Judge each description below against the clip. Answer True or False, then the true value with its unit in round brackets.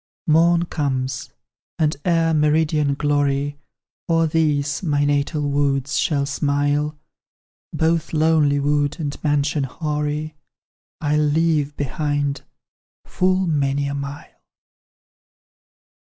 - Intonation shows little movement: True (1.6 semitones)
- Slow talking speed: True (95 wpm)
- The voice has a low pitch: False (145 Hz)